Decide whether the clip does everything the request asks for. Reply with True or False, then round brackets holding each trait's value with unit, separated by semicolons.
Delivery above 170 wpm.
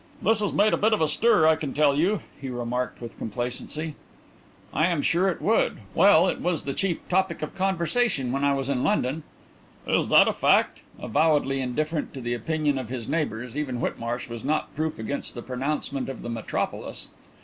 True (195 wpm)